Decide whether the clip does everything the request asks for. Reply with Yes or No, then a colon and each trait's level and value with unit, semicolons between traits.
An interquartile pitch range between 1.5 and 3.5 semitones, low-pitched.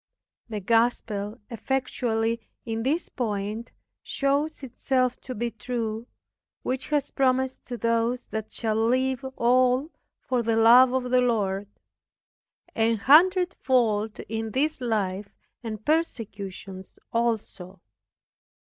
No: average, 2.8 semitones; high, 235 Hz